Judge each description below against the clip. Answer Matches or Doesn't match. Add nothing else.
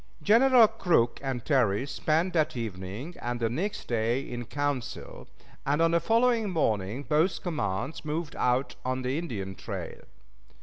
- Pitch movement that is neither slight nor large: Doesn't match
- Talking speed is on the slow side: Doesn't match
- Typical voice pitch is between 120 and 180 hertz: Matches